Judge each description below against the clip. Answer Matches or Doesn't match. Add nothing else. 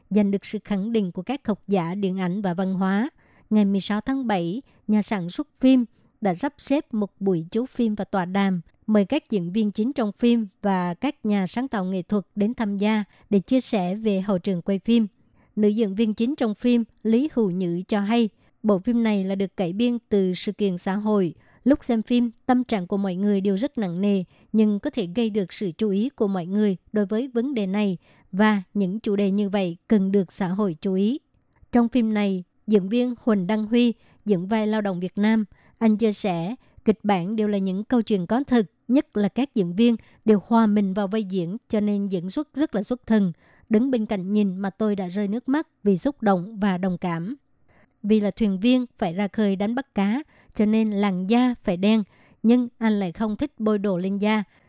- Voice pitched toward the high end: Matches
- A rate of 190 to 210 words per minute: Doesn't match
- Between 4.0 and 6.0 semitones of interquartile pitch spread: Doesn't match